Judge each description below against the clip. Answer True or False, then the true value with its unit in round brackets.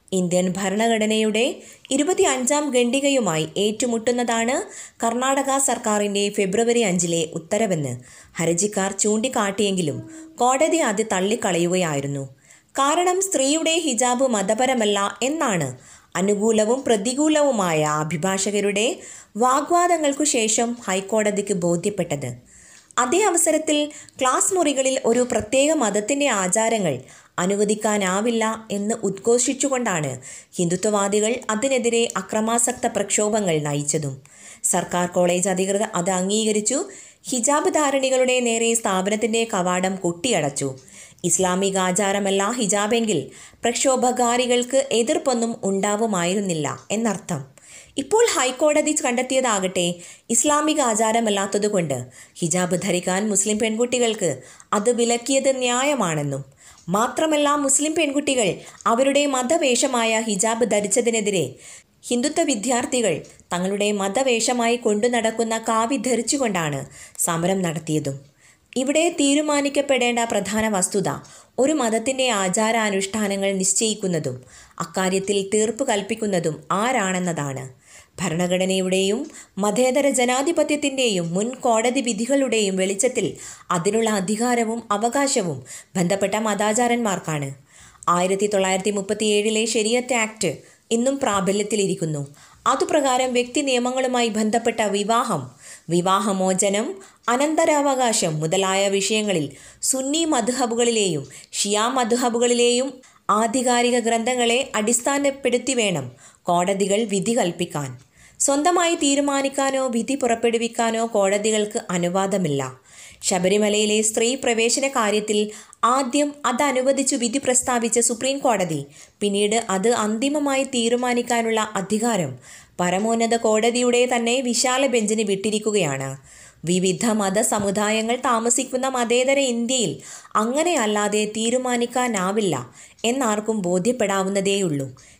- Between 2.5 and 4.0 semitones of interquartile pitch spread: False (4.8 semitones)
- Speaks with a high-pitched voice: True (220 Hz)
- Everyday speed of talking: True (80 wpm)